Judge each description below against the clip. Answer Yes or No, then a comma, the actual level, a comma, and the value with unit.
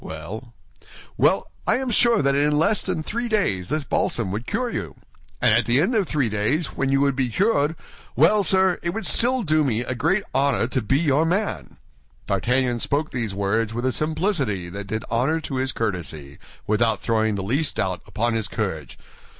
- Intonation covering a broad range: Yes, wide, 6.9 semitones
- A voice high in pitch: No, low, 135 Hz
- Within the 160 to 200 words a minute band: Yes, average, 190 wpm